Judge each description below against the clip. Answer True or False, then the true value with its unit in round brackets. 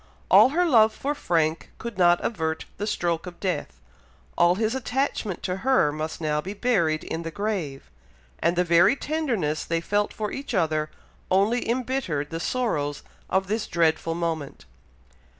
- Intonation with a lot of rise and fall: True (5.8 semitones)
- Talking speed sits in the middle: True (160 wpm)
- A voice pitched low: False (180 Hz)